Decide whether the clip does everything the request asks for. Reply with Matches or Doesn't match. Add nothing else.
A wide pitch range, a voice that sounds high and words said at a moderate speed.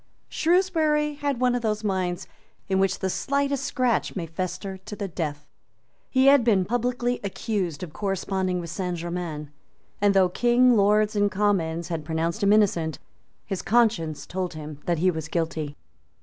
Matches